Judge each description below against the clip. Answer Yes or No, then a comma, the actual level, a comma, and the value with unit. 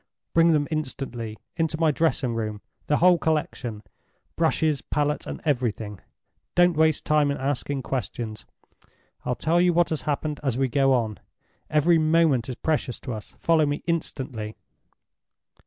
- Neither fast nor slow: Yes, average, 145 wpm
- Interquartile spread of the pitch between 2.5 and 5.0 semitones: Yes, average, 4.4 semitones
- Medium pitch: Yes, medium, 145 Hz